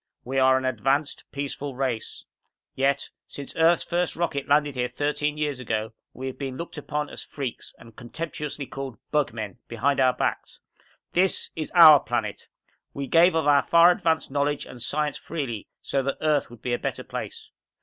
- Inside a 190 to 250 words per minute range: No, average, 180 wpm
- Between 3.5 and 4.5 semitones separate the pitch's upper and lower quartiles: No, average, 2.8 semitones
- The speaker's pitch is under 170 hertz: Yes, medium, 140 Hz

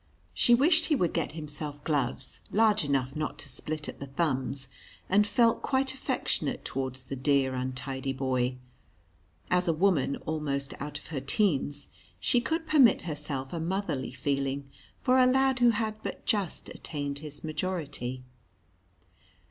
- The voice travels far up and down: Yes, wide, 7.2 semitones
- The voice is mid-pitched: Yes, medium, 150 Hz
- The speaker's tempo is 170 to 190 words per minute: No, average, 150 wpm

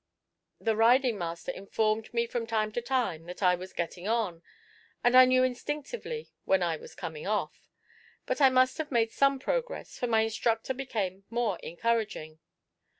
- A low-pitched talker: No, high, 225 Hz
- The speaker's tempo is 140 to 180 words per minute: Yes, average, 165 wpm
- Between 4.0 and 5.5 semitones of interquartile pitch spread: Yes, average, 5.1 semitones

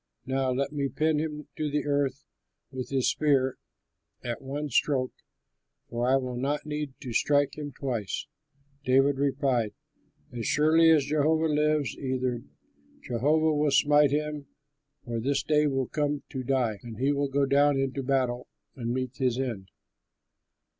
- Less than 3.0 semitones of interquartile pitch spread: Yes, narrow, 2.4 semitones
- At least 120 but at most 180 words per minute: Yes, average, 155 wpm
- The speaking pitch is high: No, medium, 140 Hz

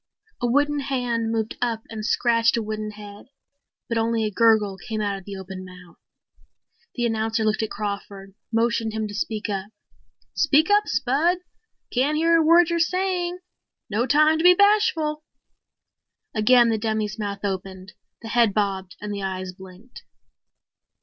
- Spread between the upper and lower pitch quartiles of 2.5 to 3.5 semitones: No, average, 5.0 semitones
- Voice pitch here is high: Yes, high, 225 Hz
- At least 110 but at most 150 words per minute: No, average, 160 wpm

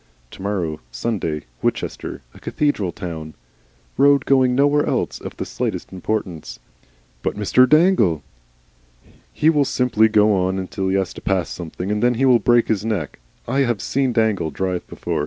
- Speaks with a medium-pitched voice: No, low, 105 Hz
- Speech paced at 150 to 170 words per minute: Yes, average, 165 wpm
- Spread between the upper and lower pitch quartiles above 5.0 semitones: Yes, wide, 5.6 semitones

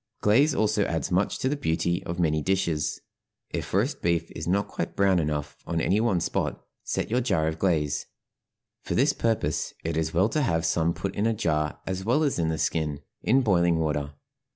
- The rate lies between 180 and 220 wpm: Yes, average, 200 wpm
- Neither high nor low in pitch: No, very low, 85 Hz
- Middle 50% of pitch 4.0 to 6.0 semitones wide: Yes, average, 4.7 semitones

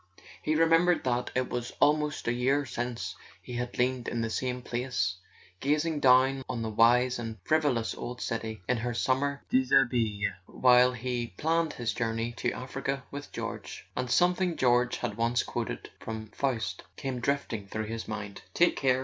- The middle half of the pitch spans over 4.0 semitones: No, average, 2.8 semitones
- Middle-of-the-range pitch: No, low, 125 Hz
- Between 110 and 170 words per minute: Yes, average, 165 wpm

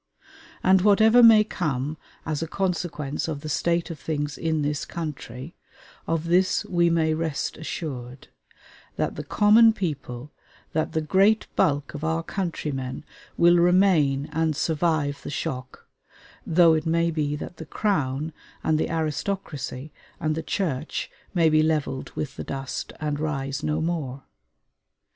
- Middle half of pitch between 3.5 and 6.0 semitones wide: No, average, 3.0 semitones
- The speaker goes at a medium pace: Yes, average, 145 wpm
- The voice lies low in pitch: No, medium, 155 Hz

